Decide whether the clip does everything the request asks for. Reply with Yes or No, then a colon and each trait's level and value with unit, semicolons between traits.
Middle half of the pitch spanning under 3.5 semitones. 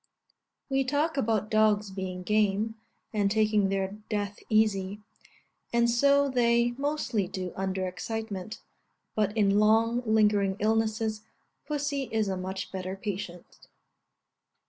Yes: average, 3.0 semitones